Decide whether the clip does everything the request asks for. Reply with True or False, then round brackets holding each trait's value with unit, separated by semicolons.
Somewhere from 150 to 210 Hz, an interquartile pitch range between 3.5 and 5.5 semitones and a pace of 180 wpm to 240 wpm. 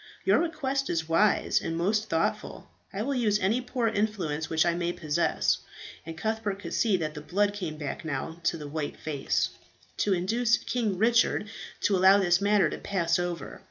True (190 Hz; 4.8 semitones; 185 wpm)